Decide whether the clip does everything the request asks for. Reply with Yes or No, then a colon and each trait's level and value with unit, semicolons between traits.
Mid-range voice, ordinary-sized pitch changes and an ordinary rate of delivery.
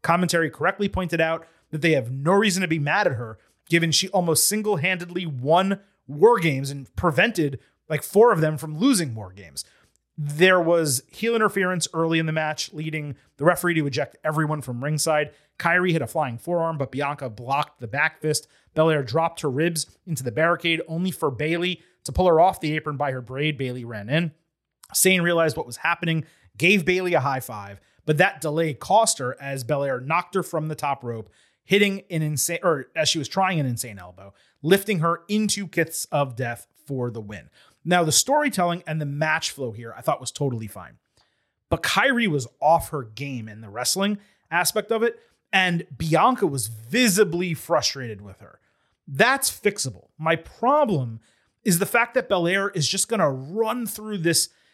Yes: medium, 160 Hz; average, 4.9 semitones; average, 185 wpm